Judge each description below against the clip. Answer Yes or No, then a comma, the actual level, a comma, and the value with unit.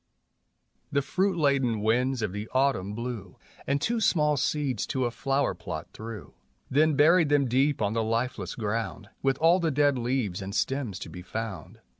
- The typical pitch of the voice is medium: No, low, 130 Hz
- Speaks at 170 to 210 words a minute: Yes, average, 175 wpm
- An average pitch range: Yes, average, 4.6 semitones